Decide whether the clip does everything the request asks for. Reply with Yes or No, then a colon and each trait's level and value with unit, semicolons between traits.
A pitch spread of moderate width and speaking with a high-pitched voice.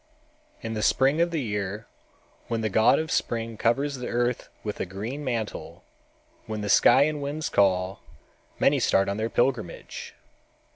No: average, 4.7 semitones; low, 115 Hz